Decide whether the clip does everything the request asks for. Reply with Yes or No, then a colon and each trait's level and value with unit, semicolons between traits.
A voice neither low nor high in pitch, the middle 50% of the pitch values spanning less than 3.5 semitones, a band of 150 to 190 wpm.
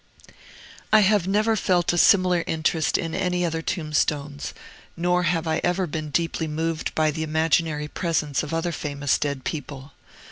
Yes: medium, 160 Hz; average, 2.7 semitones; average, 155 wpm